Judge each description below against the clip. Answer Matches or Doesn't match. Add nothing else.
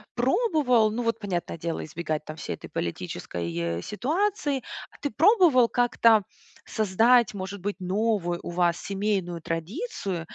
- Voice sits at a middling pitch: Doesn't match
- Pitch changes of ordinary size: Doesn't match